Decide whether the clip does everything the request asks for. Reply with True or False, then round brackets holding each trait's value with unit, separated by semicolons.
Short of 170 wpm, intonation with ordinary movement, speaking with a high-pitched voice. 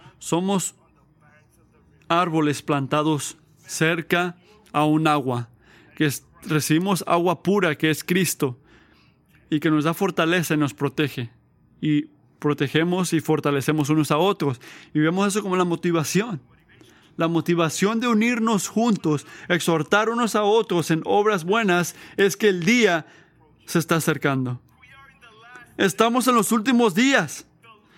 False (130 wpm; 4.3 semitones; 165 Hz)